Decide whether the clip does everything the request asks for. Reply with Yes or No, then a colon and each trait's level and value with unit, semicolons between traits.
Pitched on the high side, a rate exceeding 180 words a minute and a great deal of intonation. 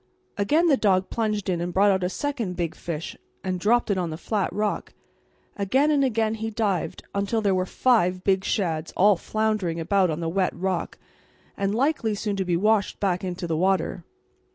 No: high, 195 Hz; average, 200 wpm; average, 3.3 semitones